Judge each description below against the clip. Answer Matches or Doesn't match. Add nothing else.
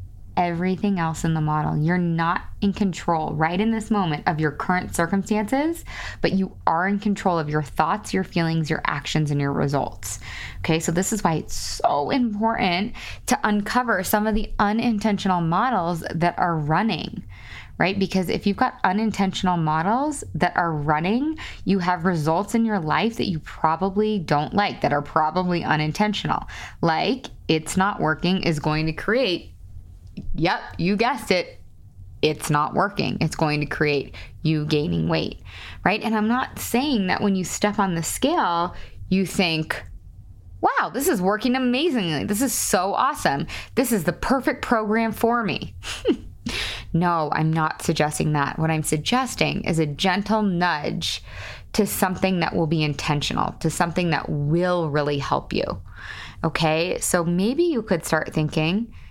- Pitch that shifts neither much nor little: Matches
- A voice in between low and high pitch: Matches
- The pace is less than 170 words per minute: Matches